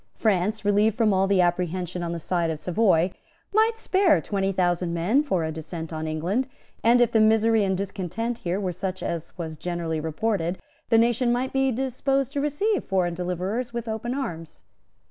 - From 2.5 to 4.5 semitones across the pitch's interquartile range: No, wide, 5.5 semitones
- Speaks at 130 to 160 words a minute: No, average, 180 wpm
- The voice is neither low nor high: No, high, 195 Hz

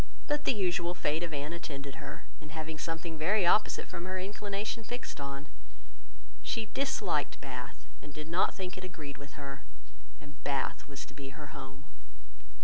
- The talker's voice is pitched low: No, medium, 155 Hz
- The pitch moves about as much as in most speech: Yes, average, 4.7 semitones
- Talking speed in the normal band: Yes, average, 170 wpm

